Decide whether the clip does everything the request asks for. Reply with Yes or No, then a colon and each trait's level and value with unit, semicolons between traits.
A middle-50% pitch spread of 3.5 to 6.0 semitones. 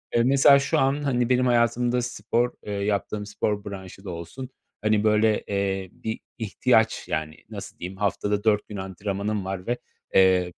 Yes: average, 3.8 semitones